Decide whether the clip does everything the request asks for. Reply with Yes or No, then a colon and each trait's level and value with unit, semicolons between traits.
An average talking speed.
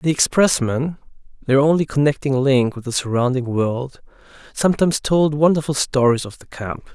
No: slow, 130 wpm